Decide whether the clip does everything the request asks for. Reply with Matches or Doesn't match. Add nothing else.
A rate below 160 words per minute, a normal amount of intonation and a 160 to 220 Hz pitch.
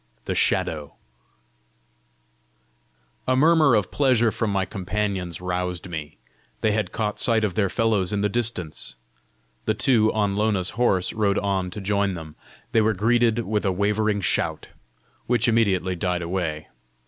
Doesn't match